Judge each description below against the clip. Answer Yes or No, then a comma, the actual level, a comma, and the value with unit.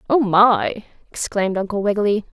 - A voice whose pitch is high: Yes, high, 210 Hz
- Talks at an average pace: No, slow, 125 wpm